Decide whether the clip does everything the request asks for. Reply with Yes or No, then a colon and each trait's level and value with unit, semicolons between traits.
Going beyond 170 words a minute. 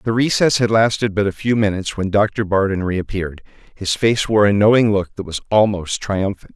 Yes: average, 200 wpm